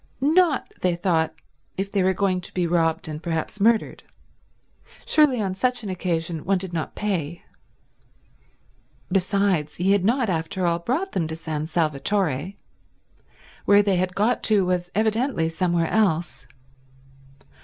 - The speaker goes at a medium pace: Yes, average, 145 wpm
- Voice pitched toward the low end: No, medium, 185 Hz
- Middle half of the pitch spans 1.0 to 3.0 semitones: No, average, 3.9 semitones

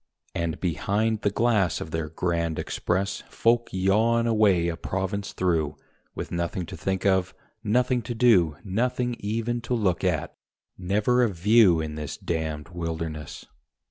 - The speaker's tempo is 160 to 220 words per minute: No, average, 145 wpm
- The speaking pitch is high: No, very low, 95 Hz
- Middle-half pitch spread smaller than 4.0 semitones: No, average, 5.1 semitones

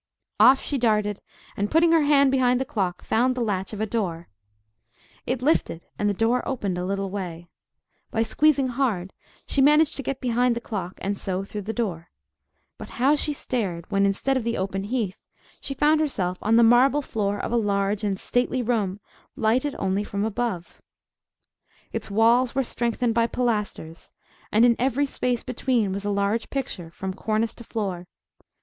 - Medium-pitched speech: No, high, 225 Hz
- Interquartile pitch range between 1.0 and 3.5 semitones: No, average, 4.3 semitones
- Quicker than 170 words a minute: Yes, average, 180 wpm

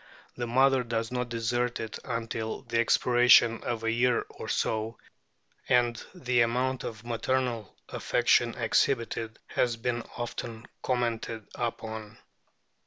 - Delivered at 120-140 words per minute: Yes, slow, 135 wpm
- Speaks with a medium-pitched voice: No, low, 120 Hz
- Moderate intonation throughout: No, narrow, 1.5 semitones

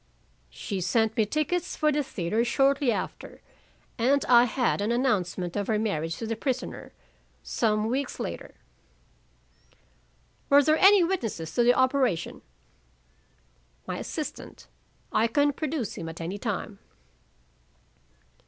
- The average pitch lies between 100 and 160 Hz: No, high, 235 Hz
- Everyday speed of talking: No, slow, 125 wpm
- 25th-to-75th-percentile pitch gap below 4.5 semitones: No, wide, 5.4 semitones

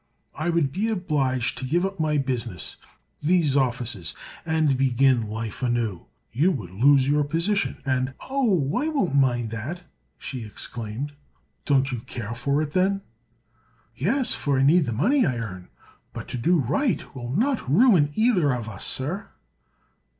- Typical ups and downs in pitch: No, wide, 6.3 semitones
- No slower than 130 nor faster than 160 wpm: Yes, average, 150 wpm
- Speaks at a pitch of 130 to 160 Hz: Yes, medium, 140 Hz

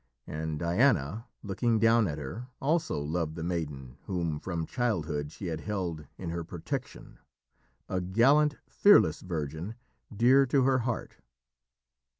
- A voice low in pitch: Yes, very low, 90 Hz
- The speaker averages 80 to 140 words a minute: Yes, slow, 135 wpm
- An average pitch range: No, wide, 6.9 semitones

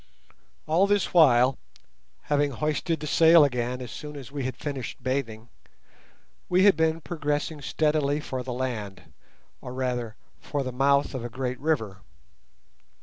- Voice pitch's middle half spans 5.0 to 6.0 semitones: No, average, 3.5 semitones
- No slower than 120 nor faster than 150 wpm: Yes, average, 145 wpm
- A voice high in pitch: No, medium, 140 Hz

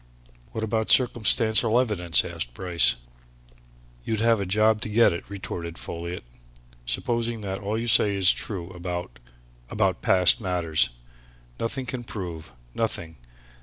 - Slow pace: Yes, slow, 130 wpm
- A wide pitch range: No, average, 4.4 semitones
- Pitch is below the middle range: Yes, low, 100 Hz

